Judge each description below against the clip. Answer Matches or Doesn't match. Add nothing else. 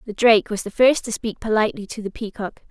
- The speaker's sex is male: Doesn't match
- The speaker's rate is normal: Doesn't match